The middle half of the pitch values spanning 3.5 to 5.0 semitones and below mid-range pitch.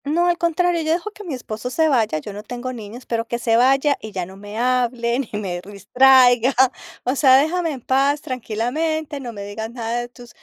No: average, 4.2 semitones; very high, 250 Hz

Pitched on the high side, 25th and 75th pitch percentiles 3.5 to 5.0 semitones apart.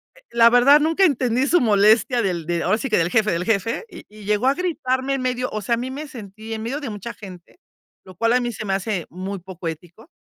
Yes: high, 225 Hz; average, 4.7 semitones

